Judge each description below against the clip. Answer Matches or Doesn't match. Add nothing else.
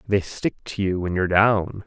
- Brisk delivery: Matches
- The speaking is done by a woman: Doesn't match